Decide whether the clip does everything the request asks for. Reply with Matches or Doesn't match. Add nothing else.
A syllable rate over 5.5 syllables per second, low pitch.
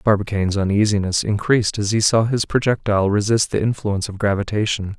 Matches